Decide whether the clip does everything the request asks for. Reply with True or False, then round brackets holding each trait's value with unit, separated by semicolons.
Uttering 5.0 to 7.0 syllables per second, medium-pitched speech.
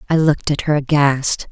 True (5.3 syllables/s; 145 Hz)